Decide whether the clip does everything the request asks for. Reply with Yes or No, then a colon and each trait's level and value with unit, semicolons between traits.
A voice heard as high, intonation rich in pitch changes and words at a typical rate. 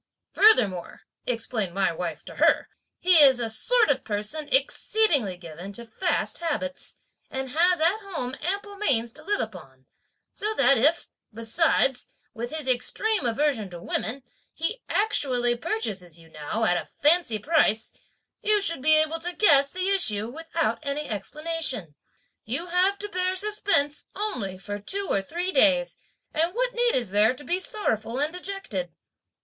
Yes: very high, 280 Hz; wide, 8.5 semitones; average, 155 wpm